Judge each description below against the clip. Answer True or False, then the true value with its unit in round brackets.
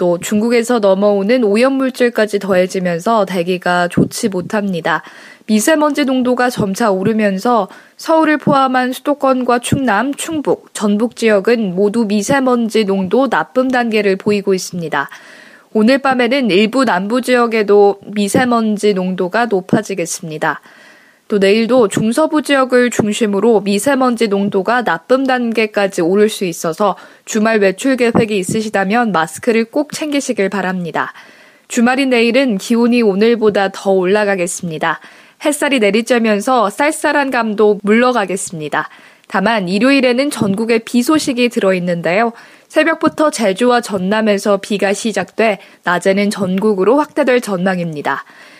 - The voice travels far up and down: False (4.2 semitones)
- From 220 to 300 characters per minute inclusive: False (320 characters per minute)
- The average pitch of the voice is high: True (220 Hz)